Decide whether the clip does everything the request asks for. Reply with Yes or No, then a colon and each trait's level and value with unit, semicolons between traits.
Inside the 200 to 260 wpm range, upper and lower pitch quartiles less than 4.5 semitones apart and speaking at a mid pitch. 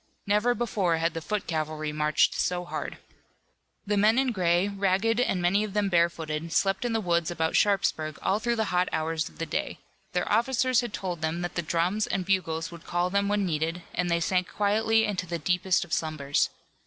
Yes: fast, 205 wpm; average, 3.9 semitones; medium, 180 Hz